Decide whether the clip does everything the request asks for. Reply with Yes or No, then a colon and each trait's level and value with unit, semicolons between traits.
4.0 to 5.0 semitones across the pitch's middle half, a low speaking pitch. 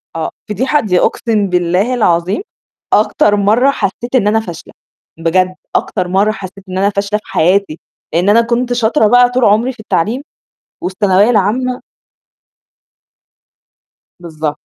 No: average, 4.4 semitones; high, 205 Hz